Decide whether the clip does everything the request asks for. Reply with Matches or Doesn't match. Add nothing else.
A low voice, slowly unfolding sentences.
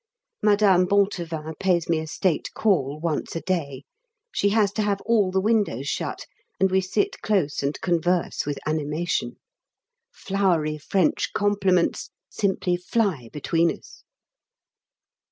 Doesn't match